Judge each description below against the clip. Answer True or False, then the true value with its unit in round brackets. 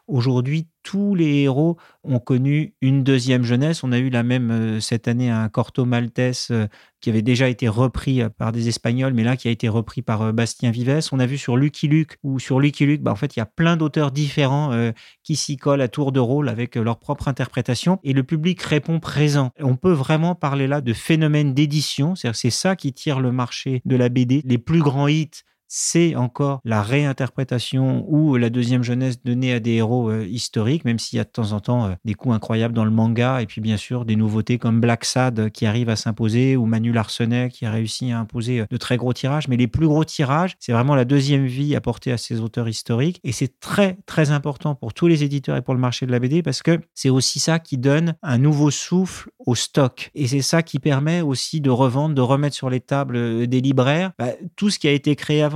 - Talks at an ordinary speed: False (235 wpm)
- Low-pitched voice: True (130 Hz)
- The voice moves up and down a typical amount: True (3.6 semitones)